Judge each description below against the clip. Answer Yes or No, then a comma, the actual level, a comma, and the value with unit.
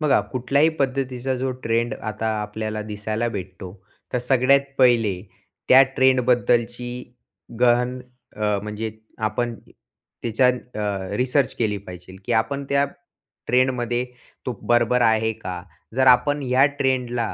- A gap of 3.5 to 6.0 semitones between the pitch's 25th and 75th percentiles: No, average, 3.0 semitones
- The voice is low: Yes, low, 120 Hz